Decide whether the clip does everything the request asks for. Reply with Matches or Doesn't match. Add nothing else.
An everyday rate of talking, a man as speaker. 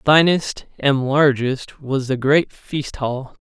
Matches